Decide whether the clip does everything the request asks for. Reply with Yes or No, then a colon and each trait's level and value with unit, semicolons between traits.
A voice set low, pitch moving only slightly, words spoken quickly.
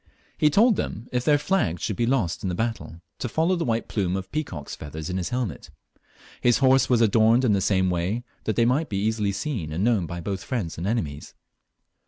No: low, 110 Hz; wide, 5.4 semitones; fast, 220 wpm